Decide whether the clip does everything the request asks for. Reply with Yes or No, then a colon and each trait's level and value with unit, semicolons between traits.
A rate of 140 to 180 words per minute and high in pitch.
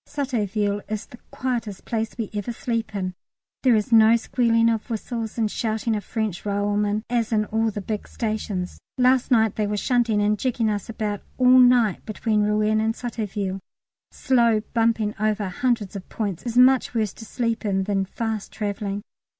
Yes: average, 175 wpm; high, 220 Hz